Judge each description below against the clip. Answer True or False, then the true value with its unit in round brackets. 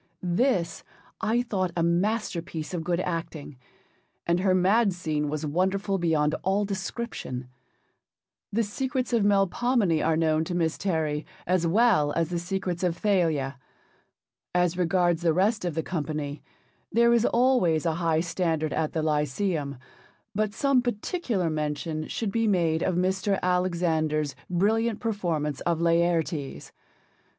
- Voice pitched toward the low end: False (175 Hz)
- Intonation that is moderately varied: True (4.1 semitones)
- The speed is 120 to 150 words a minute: True (140 wpm)